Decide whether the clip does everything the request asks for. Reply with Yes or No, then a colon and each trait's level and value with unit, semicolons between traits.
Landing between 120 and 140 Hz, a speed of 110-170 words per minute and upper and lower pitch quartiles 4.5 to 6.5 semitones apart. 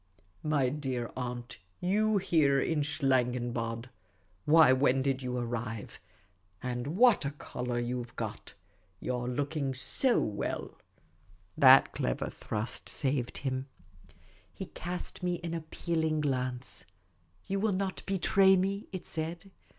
Yes: low, 135 Hz; slow, 135 wpm; wide, 5.4 semitones